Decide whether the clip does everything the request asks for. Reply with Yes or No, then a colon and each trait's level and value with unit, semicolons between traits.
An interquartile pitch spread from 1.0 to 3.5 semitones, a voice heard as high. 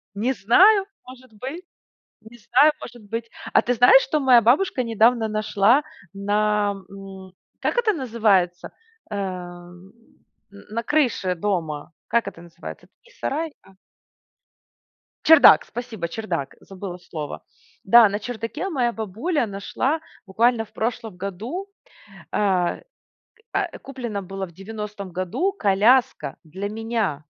No: average, 4.3 semitones; high, 215 Hz